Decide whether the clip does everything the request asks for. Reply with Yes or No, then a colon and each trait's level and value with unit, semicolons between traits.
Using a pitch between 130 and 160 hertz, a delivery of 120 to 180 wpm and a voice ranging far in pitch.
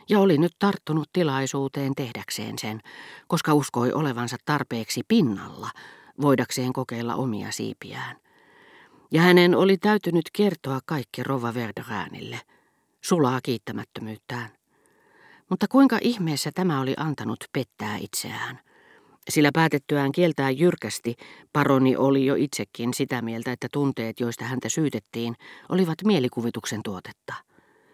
No: medium, 140 Hz; average, 110 wpm; wide, 6.1 semitones